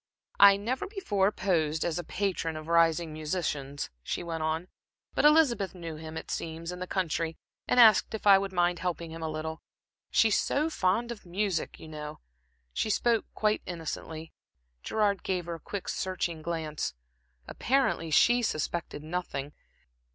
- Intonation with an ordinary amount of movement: Yes, average, 4.0 semitones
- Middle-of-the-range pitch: Yes, medium, 175 Hz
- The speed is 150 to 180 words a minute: Yes, average, 160 wpm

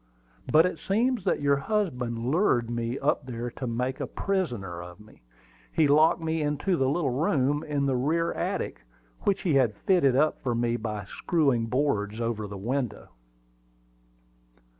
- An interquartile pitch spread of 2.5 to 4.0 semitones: No, average, 5.1 semitones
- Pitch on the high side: No, low, 135 Hz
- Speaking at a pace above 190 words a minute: No, average, 160 wpm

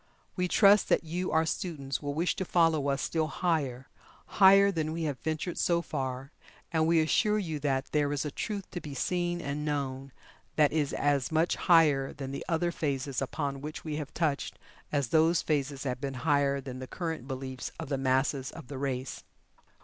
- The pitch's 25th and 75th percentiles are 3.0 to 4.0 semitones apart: Yes, average, 3.3 semitones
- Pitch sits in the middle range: Yes, medium, 150 Hz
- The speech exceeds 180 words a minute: Yes, average, 195 wpm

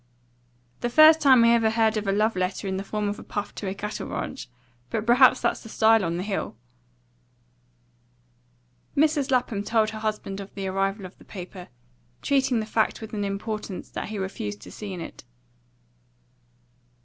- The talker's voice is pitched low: No, high, 215 Hz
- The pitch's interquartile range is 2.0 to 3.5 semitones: Yes, average, 2.8 semitones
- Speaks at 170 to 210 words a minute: Yes, average, 185 wpm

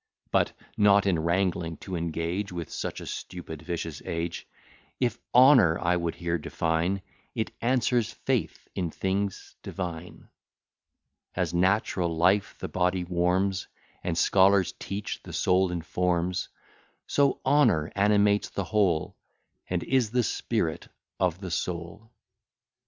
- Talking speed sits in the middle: No, slow, 125 wpm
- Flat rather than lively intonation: No, average, 3.1 semitones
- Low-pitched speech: Yes, very low, 90 Hz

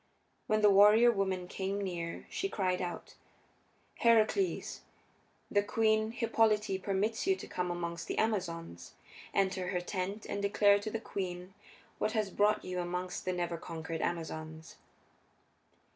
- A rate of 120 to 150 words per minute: Yes, average, 140 wpm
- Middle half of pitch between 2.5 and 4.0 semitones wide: Yes, average, 3.2 semitones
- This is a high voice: Yes, high, 195 Hz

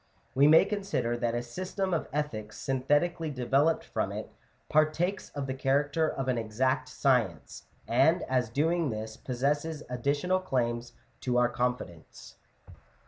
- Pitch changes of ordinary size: Yes, average, 4.3 semitones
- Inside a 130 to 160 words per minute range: Yes, average, 145 wpm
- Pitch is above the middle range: No, low, 135 Hz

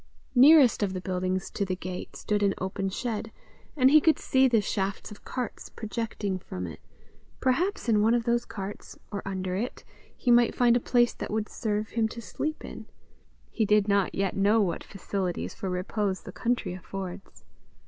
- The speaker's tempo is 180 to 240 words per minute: Yes, average, 185 wpm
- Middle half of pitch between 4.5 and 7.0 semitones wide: No, average, 3.8 semitones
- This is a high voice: Yes, high, 210 Hz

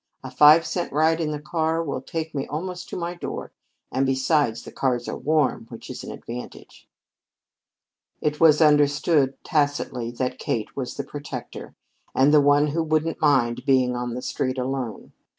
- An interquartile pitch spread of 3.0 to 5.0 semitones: Yes, average, 3.3 semitones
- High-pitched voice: No, medium, 145 Hz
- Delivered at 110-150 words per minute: No, average, 170 wpm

